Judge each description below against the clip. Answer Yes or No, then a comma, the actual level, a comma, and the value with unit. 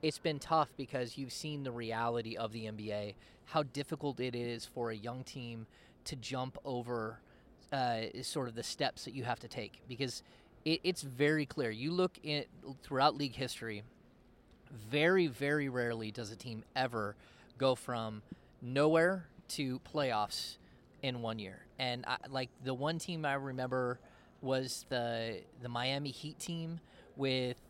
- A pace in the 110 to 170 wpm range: Yes, average, 160 wpm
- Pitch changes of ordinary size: Yes, average, 3.7 semitones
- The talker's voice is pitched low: Yes, low, 130 Hz